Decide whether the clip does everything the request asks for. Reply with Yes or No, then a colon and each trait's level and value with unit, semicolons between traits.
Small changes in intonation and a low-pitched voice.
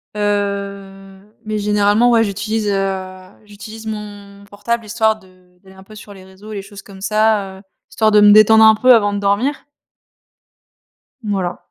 No: narrow, 1.5 semitones; high, 205 Hz